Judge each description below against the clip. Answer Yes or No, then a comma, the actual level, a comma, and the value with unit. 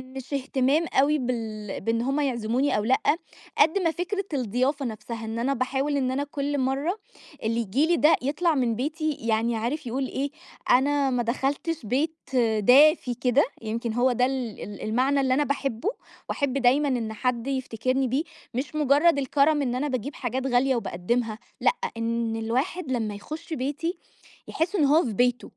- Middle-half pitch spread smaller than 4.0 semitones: Yes, average, 3.6 semitones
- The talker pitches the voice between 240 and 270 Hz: Yes, very high, 260 Hz